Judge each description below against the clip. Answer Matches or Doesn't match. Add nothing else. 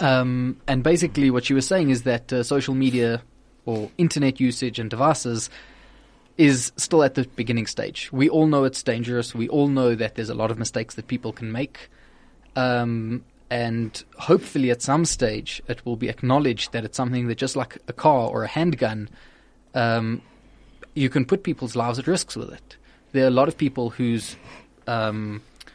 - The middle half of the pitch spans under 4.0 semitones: Matches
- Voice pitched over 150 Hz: Doesn't match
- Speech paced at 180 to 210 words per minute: Matches